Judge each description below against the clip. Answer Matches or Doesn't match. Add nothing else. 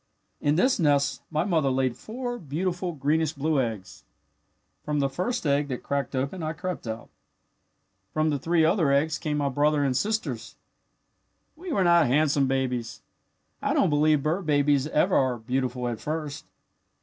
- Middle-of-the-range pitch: Matches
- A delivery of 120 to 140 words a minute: Doesn't match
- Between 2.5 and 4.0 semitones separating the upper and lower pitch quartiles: Matches